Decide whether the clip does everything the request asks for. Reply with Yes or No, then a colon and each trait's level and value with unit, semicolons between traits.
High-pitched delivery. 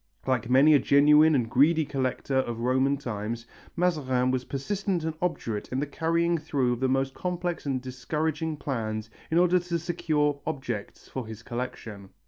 No: low, 135 Hz